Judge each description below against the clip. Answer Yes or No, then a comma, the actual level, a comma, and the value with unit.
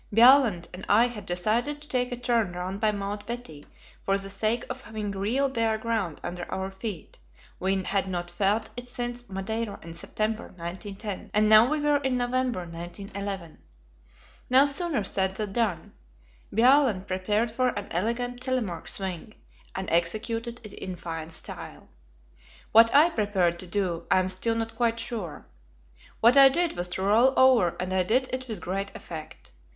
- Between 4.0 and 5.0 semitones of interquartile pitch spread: Yes, average, 4.4 semitones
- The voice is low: No, high, 215 Hz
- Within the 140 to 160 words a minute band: No, average, 170 wpm